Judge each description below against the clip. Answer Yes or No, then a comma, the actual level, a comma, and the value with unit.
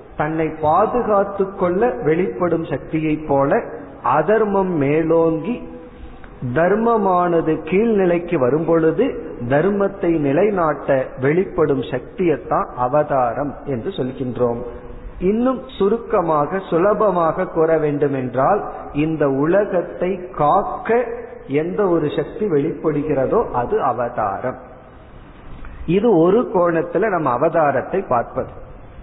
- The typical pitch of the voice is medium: Yes, medium, 160 Hz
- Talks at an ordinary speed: Yes, average, 85 wpm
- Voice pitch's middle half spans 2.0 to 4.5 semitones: No, average, 5.0 semitones